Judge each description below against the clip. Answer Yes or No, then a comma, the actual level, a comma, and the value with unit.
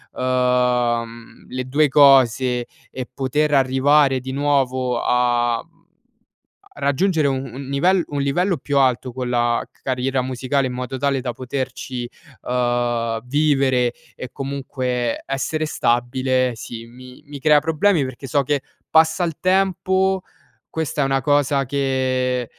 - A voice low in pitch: Yes, low, 130 Hz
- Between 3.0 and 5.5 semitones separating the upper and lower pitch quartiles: No, narrow, 2.5 semitones